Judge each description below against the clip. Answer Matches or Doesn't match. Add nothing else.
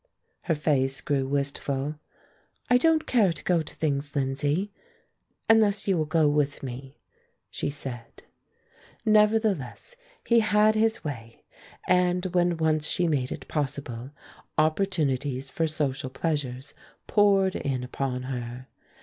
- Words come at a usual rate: Doesn't match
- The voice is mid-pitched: Matches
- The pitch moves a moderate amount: Doesn't match